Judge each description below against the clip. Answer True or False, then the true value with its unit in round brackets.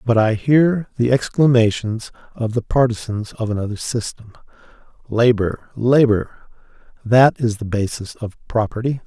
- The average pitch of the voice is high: False (115 Hz)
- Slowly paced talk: True (125 wpm)